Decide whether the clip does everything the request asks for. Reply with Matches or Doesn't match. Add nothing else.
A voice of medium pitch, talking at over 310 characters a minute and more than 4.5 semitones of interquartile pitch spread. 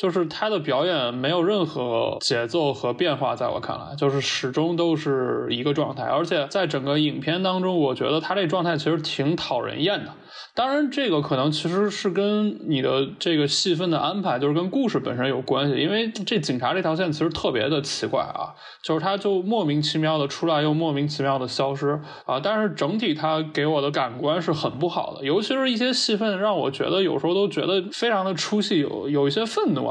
Matches